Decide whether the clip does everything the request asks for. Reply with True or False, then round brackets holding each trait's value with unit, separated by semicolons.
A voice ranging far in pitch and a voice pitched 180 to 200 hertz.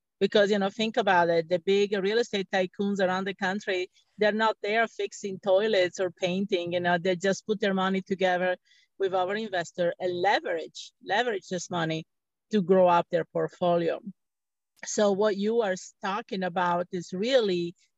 False (2.5 semitones; 190 Hz)